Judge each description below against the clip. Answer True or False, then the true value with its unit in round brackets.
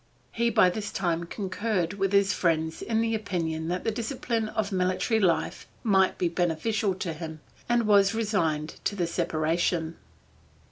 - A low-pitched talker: False (185 Hz)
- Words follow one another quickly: False (155 wpm)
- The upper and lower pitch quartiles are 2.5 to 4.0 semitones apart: False (4.4 semitones)